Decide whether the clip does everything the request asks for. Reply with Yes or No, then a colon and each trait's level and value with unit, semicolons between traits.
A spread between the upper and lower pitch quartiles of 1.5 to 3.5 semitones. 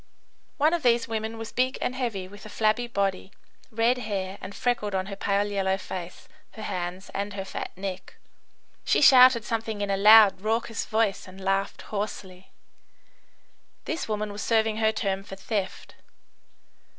Yes: narrow, 2.6 semitones